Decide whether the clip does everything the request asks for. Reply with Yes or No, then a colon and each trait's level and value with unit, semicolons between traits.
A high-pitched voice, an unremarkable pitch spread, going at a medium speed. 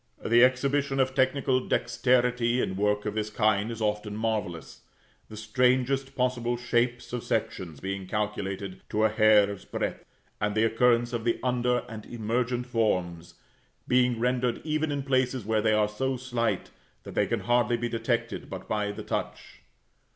No: low, 115 Hz; average, 3.0 semitones; average, 160 wpm